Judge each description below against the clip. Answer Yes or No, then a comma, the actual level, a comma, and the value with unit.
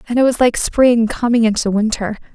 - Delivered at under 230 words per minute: Yes, fast, 205 wpm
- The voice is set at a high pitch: Yes, high, 230 Hz